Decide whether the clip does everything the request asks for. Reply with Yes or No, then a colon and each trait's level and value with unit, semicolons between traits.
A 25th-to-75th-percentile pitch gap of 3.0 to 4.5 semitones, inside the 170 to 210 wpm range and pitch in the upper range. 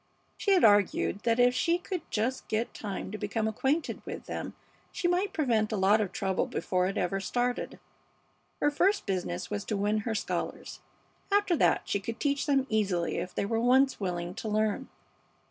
No: wide, 5.4 semitones; average, 185 wpm; high, 220 Hz